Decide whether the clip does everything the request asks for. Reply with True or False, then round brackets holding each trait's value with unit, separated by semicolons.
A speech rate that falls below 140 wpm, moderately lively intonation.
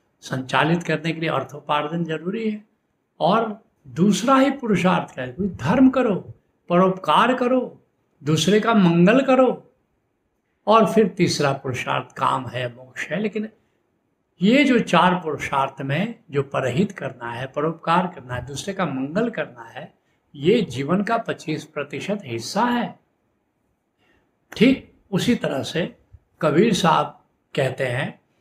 False (130 wpm; 7.5 semitones)